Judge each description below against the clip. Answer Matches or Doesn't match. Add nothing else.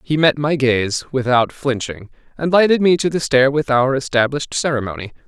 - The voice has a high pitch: Doesn't match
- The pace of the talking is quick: Doesn't match